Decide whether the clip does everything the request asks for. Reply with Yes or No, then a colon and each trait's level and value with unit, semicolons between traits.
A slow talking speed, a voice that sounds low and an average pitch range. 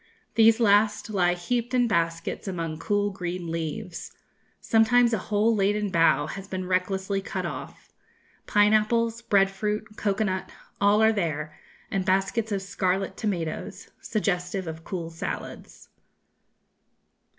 No: slow, 130 wpm; high, 195 Hz; average, 3.2 semitones